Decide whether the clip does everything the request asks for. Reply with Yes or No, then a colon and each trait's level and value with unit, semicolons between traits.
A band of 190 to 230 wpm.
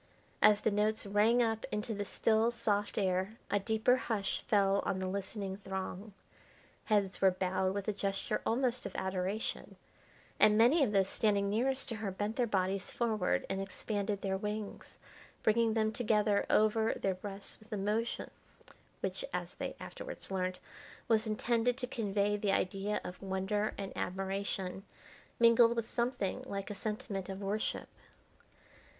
No: average, 155 wpm